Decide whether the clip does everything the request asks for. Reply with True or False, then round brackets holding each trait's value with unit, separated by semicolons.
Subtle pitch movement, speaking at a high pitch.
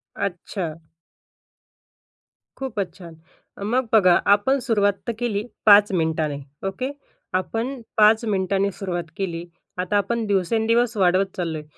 False (4.0 semitones; 200 Hz)